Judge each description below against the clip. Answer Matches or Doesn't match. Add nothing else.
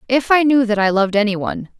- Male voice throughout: Doesn't match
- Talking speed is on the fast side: Matches